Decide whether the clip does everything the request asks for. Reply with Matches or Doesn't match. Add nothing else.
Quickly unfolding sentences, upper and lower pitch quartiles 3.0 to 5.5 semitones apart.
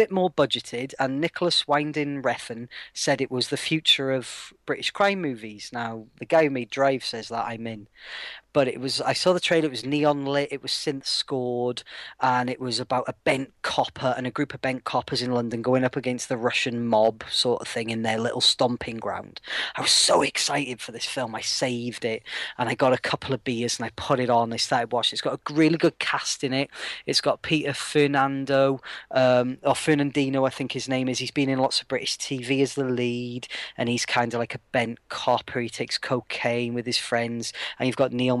Doesn't match